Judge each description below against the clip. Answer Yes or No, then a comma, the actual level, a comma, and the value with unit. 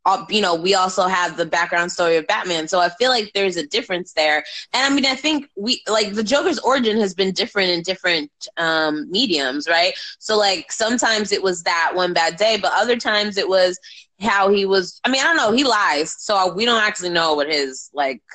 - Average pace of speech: No, fast, 225 wpm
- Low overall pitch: No, high, 190 Hz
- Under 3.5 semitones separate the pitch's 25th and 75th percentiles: No, average, 4.2 semitones